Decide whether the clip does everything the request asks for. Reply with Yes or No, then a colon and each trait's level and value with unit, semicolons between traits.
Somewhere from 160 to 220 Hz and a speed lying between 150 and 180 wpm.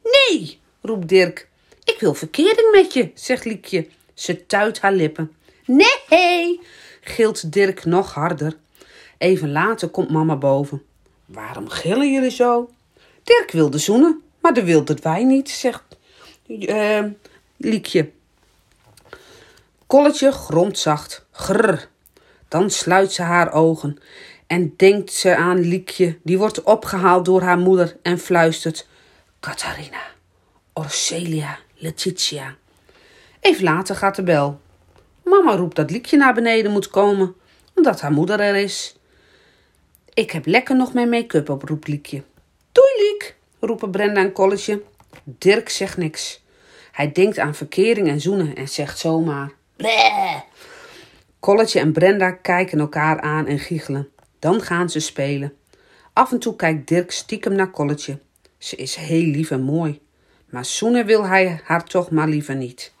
No: medium, 185 Hz; average, 140 wpm